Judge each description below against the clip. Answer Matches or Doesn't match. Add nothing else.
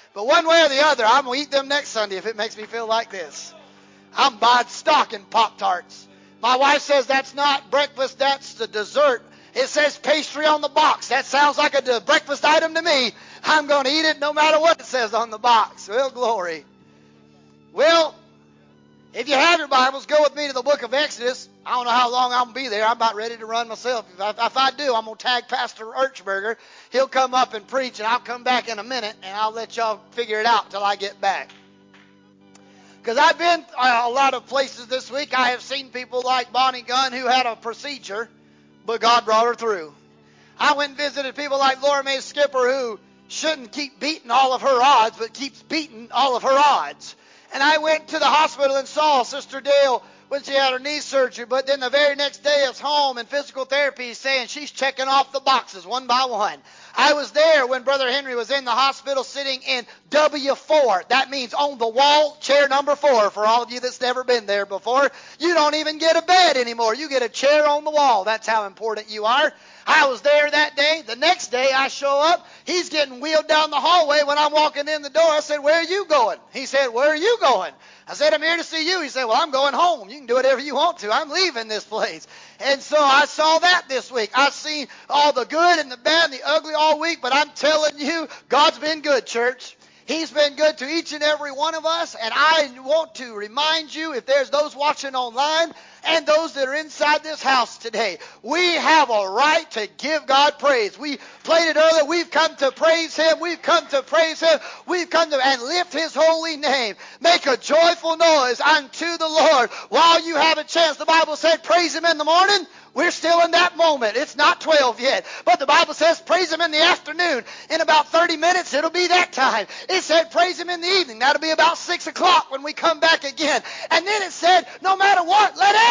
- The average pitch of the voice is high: Matches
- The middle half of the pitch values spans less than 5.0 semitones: Matches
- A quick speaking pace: Matches